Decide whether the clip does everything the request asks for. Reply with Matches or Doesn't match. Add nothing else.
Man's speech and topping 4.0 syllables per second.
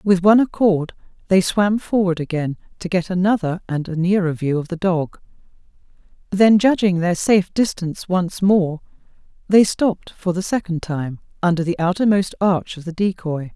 Doesn't match